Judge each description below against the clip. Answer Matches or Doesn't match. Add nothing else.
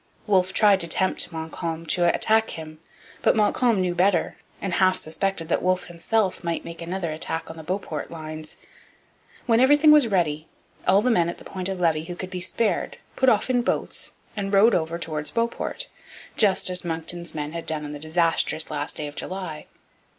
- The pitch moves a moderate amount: Matches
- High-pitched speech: Doesn't match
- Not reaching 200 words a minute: Matches